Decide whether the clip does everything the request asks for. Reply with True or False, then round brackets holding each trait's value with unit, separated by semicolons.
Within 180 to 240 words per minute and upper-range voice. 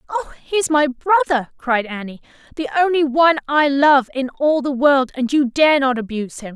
True (200 wpm; 275 Hz)